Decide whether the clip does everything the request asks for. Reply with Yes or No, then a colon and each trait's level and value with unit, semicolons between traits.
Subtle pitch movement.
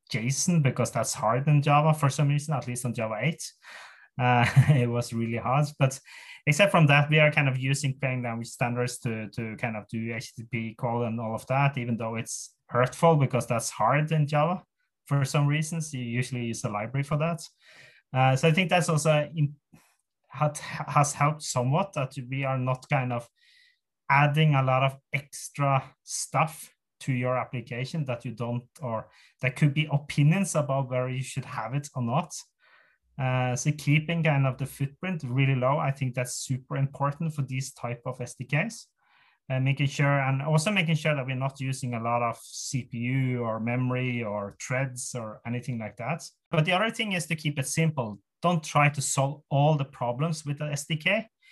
No: average, 3.5 semitones